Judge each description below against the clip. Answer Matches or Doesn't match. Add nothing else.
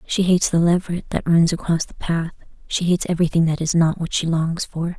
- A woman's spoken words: Matches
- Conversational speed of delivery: Doesn't match